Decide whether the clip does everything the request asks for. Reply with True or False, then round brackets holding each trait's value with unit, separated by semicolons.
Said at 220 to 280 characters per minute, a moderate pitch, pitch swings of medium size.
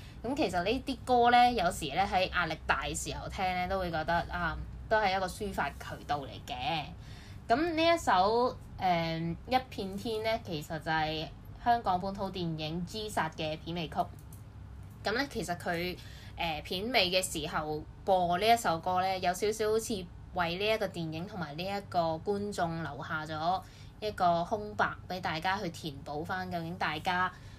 True (250 characters per minute; 180 Hz; 4.6 semitones)